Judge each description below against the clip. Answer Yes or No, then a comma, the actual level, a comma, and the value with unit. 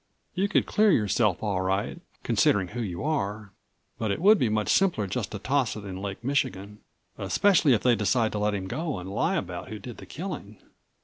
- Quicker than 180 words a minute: Yes, fast, 205 wpm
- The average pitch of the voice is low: Yes, low, 110 Hz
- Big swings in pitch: Yes, wide, 6.2 semitones